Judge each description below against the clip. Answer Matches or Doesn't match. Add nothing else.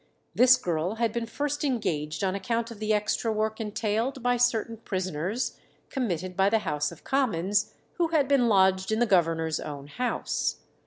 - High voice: Matches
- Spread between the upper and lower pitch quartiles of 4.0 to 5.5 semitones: Matches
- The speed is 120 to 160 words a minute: Doesn't match